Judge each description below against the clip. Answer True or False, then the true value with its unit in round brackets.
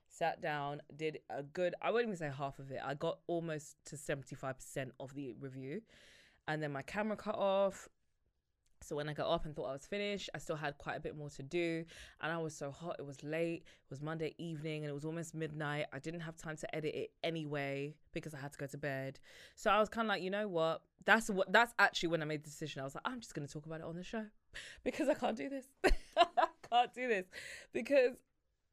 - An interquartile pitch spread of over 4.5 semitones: True (5.1 semitones)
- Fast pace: True (245 wpm)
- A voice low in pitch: False (160 Hz)